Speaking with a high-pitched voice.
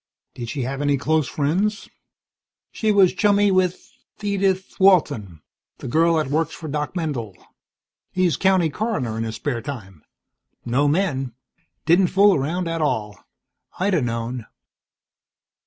No: medium, 155 Hz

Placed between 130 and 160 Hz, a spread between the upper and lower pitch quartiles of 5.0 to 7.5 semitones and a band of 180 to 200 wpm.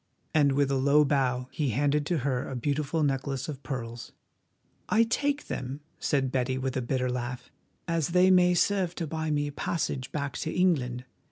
No: medium, 140 Hz; average, 3.7 semitones; average, 185 wpm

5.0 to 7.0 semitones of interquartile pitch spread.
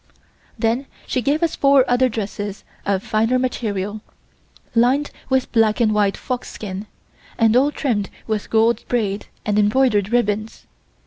No: average, 3.5 semitones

